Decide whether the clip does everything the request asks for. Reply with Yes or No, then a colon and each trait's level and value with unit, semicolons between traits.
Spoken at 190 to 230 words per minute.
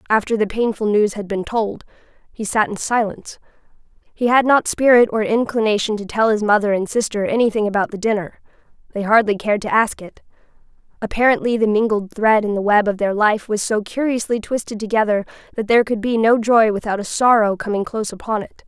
Yes: average, 195 wpm